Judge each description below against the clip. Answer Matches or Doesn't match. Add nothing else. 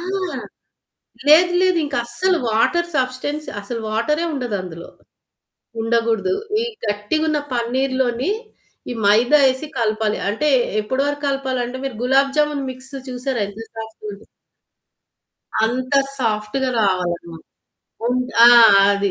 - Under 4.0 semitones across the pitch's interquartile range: Doesn't match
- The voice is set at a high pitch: Matches